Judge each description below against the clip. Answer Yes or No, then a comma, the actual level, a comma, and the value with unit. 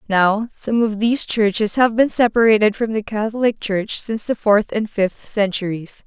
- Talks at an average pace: Yes, average, 180 wpm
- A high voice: Yes, high, 215 Hz